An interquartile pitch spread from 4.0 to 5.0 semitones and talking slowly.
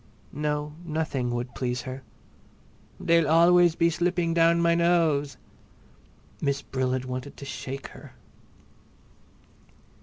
Yes: average, 4.3 semitones; slow, 115 wpm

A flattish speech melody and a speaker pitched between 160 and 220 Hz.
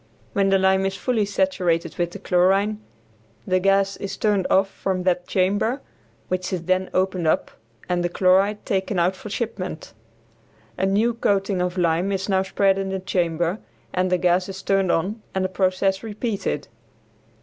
Yes: narrow, 1.5 semitones; high, 190 Hz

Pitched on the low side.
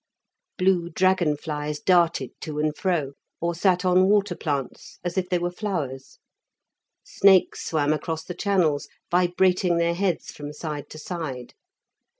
No: medium, 170 Hz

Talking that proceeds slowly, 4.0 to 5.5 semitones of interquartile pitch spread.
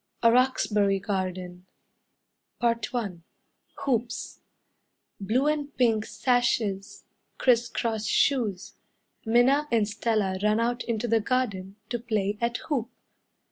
No: slow, 105 wpm; average, 3.2 semitones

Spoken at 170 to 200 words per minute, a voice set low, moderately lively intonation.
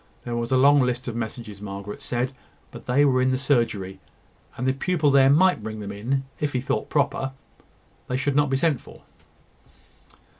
Yes: average, 190 wpm; low, 130 Hz; average, 3.1 semitones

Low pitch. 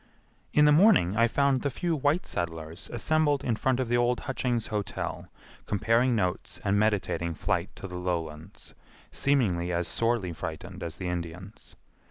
Yes: low, 105 Hz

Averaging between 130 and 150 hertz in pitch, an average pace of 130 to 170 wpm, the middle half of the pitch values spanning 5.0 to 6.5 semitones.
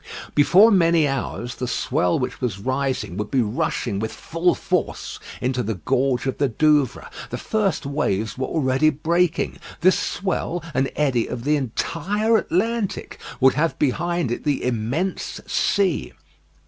Yes: medium, 140 Hz; average, 150 wpm; wide, 5.5 semitones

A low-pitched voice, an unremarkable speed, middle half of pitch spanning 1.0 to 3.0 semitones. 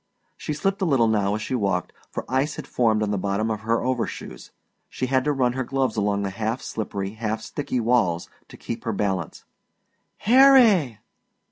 No: low, 115 Hz; average, 190 wpm; average, 4.3 semitones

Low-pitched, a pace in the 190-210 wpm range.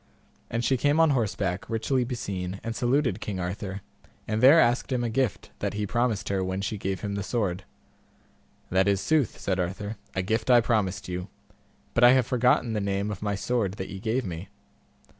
Yes: low, 105 Hz; average, 195 wpm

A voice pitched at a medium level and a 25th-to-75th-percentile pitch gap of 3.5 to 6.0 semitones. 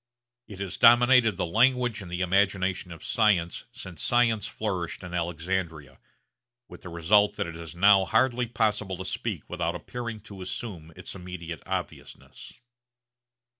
No: very low, 95 Hz; average, 4.1 semitones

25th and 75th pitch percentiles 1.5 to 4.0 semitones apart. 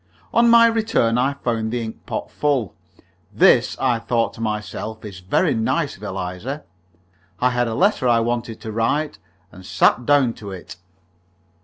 Yes: average, 3.7 semitones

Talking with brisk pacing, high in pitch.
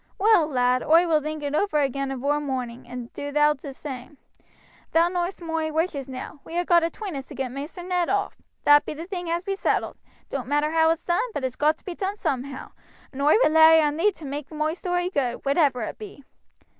Yes: fast, 230 wpm; very high, 305 Hz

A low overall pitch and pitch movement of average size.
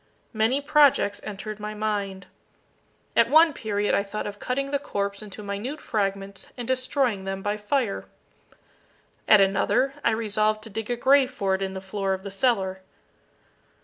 No: high, 210 Hz; average, 4.2 semitones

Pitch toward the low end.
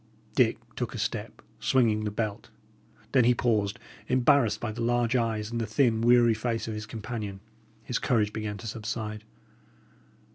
Yes: low, 115 Hz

